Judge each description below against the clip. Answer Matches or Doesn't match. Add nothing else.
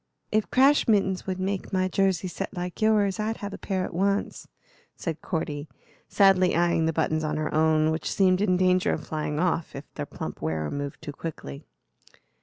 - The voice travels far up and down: Doesn't match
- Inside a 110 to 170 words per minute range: Doesn't match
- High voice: Doesn't match